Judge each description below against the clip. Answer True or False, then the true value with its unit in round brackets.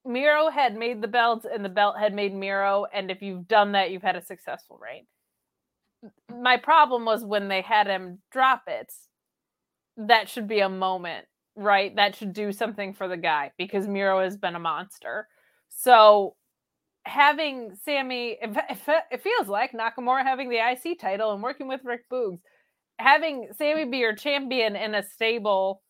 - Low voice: False (220 Hz)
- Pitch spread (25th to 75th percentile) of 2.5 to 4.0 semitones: False (4.4 semitones)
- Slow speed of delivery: False (170 wpm)